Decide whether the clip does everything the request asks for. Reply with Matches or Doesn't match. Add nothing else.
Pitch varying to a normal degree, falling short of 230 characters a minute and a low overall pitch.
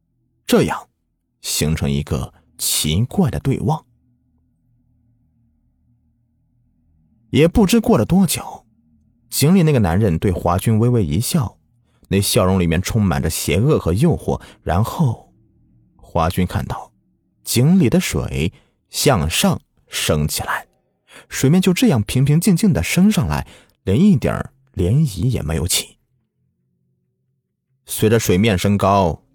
Doesn't match